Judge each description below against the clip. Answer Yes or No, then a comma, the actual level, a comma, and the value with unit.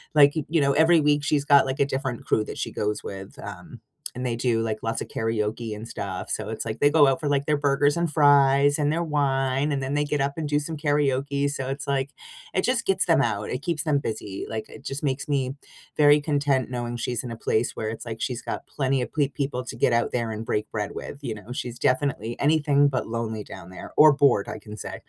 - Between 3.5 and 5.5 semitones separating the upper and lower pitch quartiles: Yes, average, 3.9 semitones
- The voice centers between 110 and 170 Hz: Yes, low, 135 Hz